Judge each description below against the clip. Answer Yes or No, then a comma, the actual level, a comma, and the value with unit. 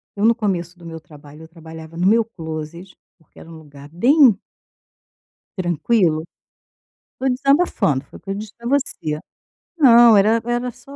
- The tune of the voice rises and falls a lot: Yes, wide, 6.6 semitones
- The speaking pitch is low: No, medium, 185 Hz